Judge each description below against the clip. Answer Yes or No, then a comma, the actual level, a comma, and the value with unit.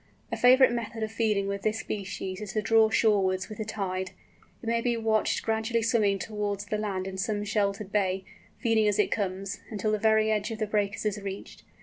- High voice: Yes, high, 210 Hz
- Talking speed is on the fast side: Yes, fast, 210 wpm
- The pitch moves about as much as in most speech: No, narrow, 1.8 semitones